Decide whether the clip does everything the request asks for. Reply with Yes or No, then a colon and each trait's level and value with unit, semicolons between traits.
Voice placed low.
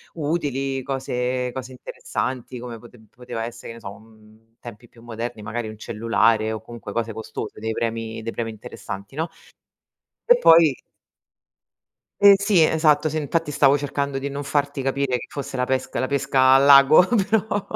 Yes: low, 130 Hz